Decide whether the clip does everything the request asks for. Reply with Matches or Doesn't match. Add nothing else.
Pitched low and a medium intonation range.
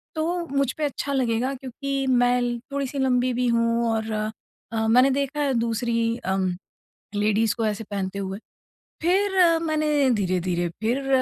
Doesn't match